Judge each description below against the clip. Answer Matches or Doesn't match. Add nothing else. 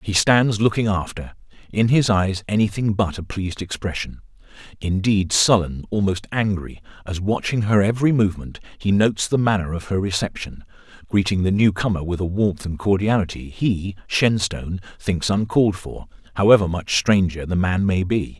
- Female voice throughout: Doesn't match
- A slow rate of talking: Doesn't match